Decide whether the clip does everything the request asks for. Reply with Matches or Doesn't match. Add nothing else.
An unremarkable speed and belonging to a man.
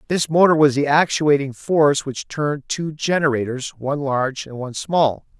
Matches